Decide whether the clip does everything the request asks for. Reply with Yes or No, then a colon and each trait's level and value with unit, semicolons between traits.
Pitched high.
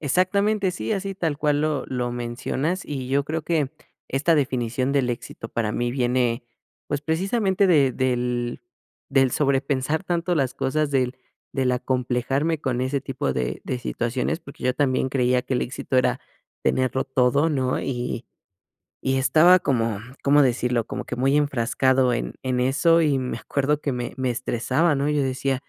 No: low, 135 Hz